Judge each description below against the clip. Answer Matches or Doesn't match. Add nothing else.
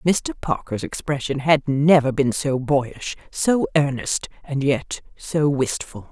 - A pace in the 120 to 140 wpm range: Matches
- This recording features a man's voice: Doesn't match